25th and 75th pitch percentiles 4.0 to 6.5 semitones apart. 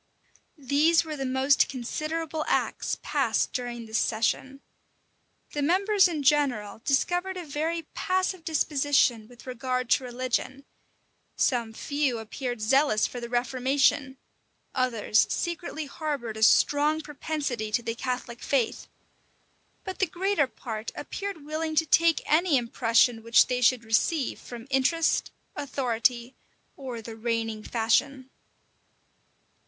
Yes: average, 4.5 semitones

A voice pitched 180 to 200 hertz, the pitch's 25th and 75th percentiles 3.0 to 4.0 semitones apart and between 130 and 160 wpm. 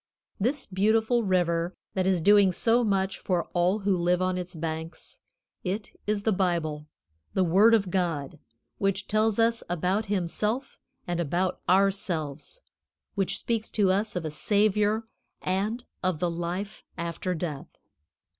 Yes: high, 190 Hz; average, 3.3 semitones; average, 145 wpm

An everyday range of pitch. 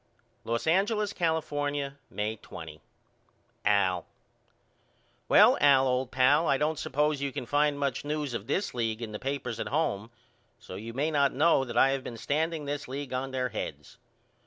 Yes: average, 4.0 semitones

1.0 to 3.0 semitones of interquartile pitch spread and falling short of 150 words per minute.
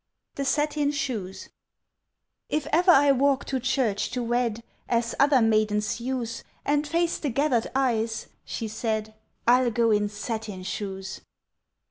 No: average, 4.2 semitones; slow, 135 wpm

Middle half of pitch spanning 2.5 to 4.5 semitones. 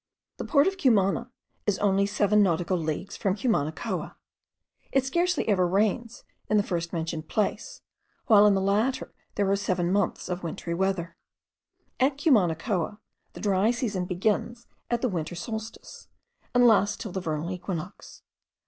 Yes: average, 4.1 semitones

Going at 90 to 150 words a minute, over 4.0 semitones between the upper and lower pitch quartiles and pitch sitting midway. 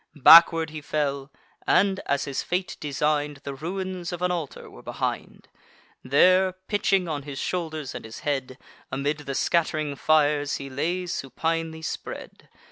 No: average, 145 wpm; average, 3.7 semitones; medium, 155 Hz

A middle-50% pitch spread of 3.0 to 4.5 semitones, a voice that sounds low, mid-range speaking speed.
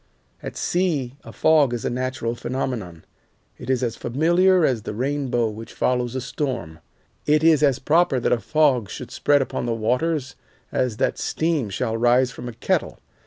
Yes: average, 3.8 semitones; low, 130 Hz; average, 175 wpm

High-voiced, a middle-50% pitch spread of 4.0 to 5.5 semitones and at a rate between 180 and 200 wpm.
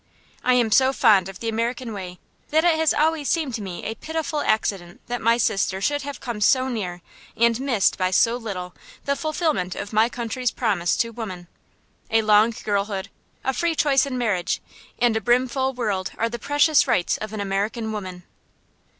Yes: high, 230 Hz; average, 4.7 semitones; average, 185 wpm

